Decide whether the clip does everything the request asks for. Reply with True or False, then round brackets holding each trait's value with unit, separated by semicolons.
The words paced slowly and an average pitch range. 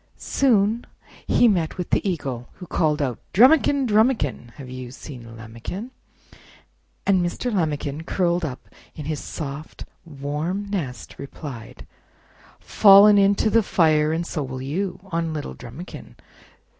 False (130 wpm; 6.2 semitones)